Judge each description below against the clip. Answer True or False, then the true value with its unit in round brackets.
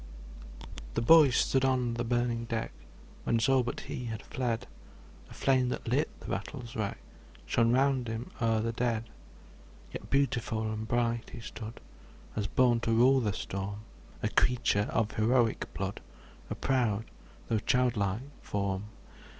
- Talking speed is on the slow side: False (150 wpm)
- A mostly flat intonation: True (2.3 semitones)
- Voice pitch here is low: True (115 Hz)